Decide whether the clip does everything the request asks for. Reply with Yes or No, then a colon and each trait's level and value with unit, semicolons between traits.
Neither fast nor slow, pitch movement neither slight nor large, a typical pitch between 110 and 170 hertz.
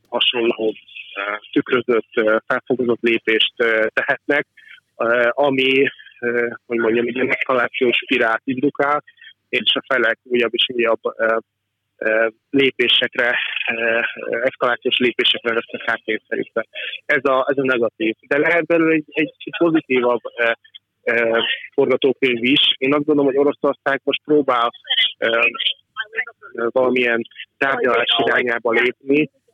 No: slow, 100 wpm; average, 4.1 semitones; low, 130 Hz